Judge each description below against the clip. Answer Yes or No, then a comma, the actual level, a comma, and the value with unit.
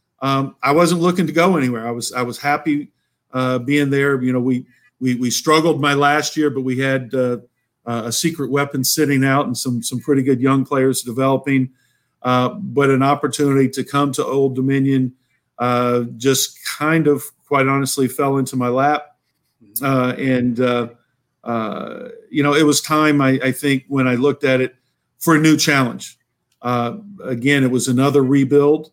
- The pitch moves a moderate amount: No, narrow, 2.2 semitones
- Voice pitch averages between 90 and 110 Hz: No, low, 135 Hz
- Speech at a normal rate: Yes, average, 180 wpm